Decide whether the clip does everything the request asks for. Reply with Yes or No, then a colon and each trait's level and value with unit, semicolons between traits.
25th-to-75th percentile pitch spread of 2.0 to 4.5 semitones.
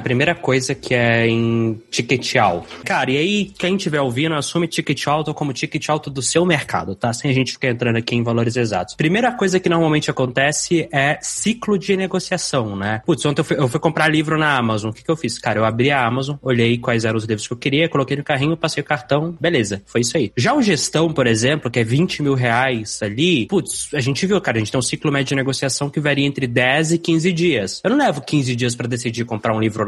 No: average, 5.1 semitones